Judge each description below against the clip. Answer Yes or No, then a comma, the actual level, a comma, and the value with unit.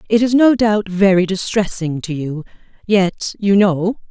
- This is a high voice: Yes, high, 195 Hz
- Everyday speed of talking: Yes, average, 160 wpm